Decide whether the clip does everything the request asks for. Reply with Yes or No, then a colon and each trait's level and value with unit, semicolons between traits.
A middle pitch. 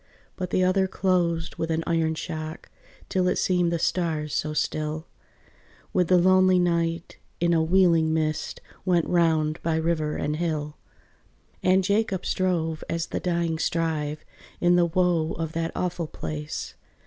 Yes: medium, 165 Hz